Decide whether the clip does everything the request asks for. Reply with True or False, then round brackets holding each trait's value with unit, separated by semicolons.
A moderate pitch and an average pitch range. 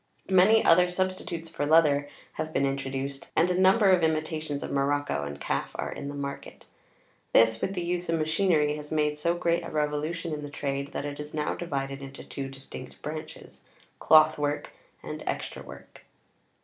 True (150 Hz; 3.1 semitones)